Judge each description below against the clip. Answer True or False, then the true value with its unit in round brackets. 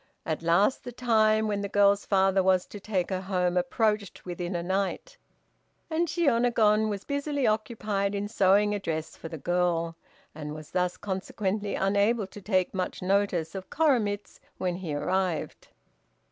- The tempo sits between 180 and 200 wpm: False (160 wpm)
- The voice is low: False (200 Hz)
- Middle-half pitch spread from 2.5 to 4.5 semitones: True (3.0 semitones)